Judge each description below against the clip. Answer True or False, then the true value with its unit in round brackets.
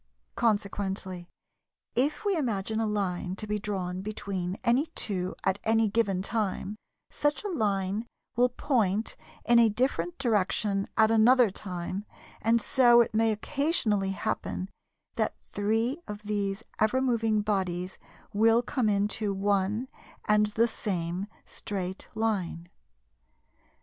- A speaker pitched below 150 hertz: False (210 Hz)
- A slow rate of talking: True (125 wpm)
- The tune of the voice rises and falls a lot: False (2.9 semitones)